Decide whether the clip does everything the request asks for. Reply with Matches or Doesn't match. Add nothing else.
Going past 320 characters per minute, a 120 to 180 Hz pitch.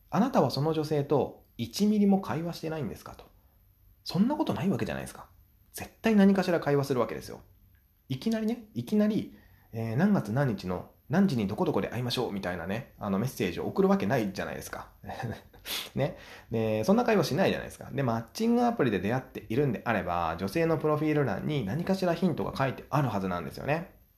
Matches